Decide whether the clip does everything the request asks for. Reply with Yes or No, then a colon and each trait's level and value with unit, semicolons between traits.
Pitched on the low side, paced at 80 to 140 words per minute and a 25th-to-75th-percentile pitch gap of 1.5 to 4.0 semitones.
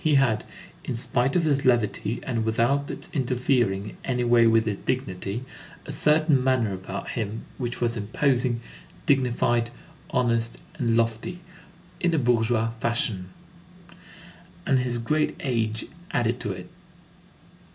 Yes: low, 120 Hz; slow, 135 wpm; narrow, 2.6 semitones